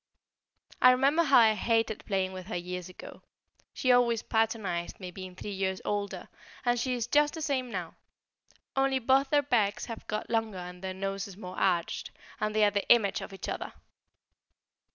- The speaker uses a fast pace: No, average, 180 wpm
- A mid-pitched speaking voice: No, high, 215 Hz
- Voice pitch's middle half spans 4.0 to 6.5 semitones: Yes, average, 4.6 semitones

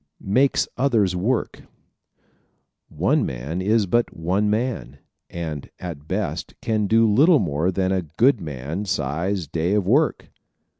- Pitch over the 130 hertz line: No, very low, 95 Hz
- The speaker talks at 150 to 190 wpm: No, average, 140 wpm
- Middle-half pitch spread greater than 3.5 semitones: Yes, wide, 5.6 semitones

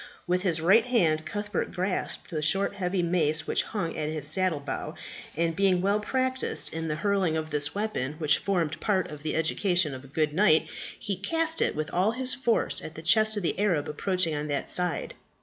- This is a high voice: No, medium, 180 Hz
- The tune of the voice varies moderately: Yes, average, 4.4 semitones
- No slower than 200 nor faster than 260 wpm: Yes, fast, 205 wpm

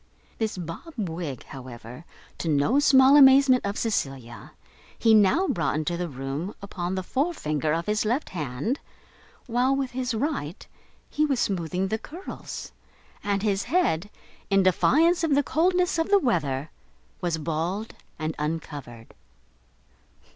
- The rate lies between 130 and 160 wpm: Yes, average, 140 wpm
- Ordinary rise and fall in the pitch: No, wide, 9.0 semitones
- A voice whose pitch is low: No, high, 195 Hz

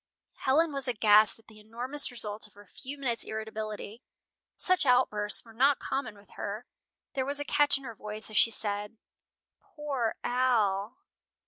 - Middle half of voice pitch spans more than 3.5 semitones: Yes, average, 4.0 semitones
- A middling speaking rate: Yes, average, 160 wpm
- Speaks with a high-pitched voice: Yes, high, 230 Hz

